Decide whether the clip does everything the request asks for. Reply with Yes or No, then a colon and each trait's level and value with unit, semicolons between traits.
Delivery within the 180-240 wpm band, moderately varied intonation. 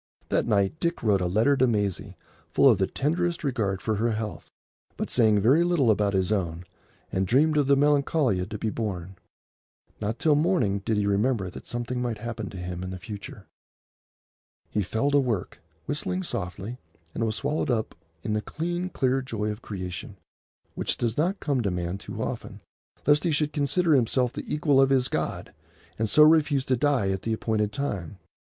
No: average, 190 wpm; wide, 5.9 semitones